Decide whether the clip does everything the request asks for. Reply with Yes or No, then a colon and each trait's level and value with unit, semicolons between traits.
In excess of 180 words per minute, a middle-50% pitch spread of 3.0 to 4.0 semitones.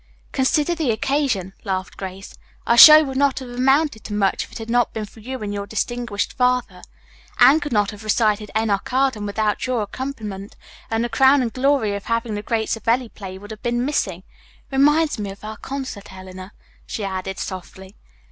No: average, 190 wpm; average, 4.4 semitones